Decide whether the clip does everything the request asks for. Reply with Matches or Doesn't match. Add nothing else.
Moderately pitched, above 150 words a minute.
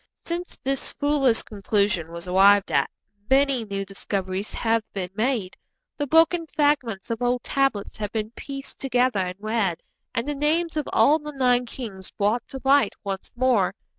Doesn't match